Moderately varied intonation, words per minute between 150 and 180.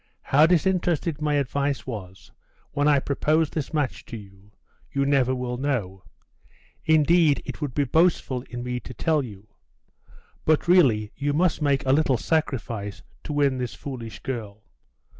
Yes: average, 4.0 semitones; average, 155 wpm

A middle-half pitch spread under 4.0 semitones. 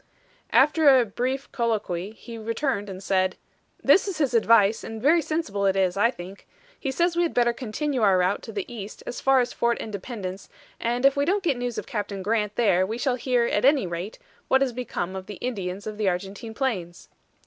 No: average, 5.0 semitones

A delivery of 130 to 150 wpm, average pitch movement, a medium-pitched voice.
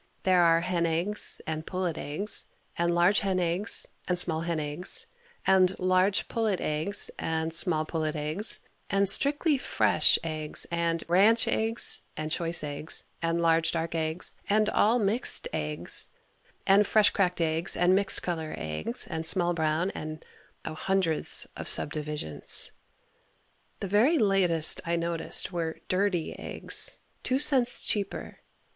Yes: average, 145 wpm; average, 3.6 semitones; medium, 175 Hz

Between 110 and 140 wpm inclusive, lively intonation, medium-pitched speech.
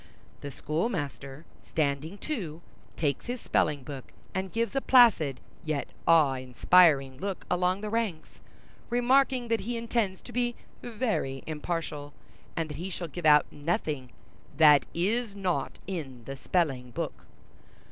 Yes: slow, 135 wpm; wide, 7.0 semitones; medium, 165 Hz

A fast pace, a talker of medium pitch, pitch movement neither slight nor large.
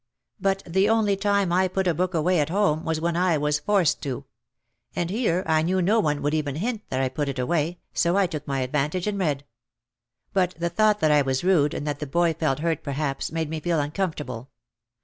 Yes: fast, 225 wpm; medium, 165 Hz; average, 4.1 semitones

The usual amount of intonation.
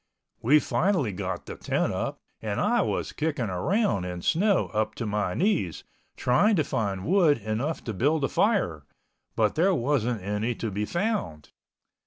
No: wide, 8.3 semitones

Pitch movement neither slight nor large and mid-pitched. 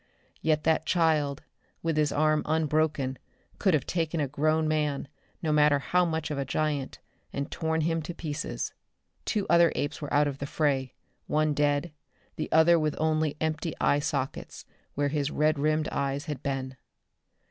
No: narrow, 1.9 semitones; medium, 150 Hz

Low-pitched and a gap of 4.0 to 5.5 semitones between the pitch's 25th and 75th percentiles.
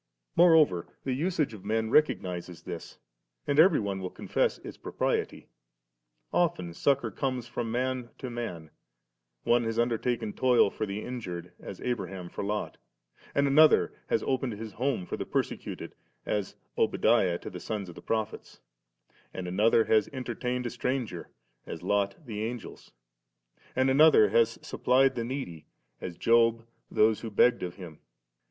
Yes: low, 115 Hz; average, 4.5 semitones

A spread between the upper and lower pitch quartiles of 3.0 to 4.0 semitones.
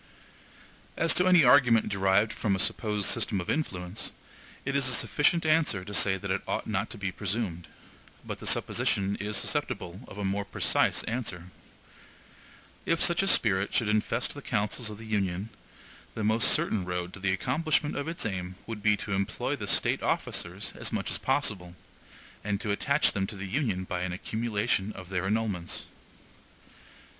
Yes: average, 3.3 semitones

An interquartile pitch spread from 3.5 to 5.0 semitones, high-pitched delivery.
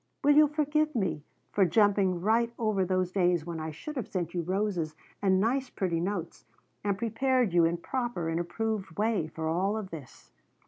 Yes: average, 4.7 semitones; high, 195 Hz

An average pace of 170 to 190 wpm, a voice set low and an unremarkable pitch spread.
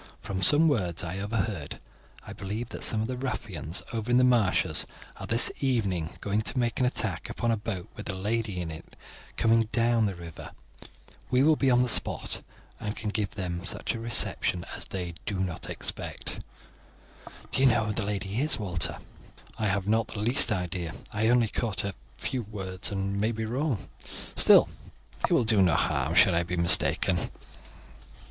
Yes: average, 185 wpm; low, 105 Hz; average, 3.9 semitones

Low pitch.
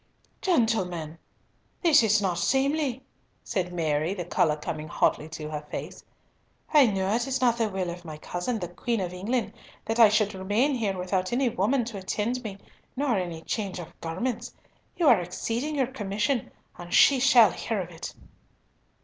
No: high, 205 Hz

